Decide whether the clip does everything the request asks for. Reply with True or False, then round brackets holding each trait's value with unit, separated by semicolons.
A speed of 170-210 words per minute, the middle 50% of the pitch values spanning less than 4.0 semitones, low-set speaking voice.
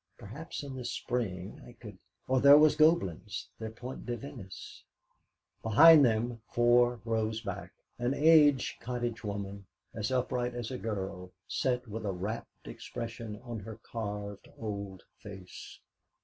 False (145 wpm; 3.4 semitones; 115 Hz)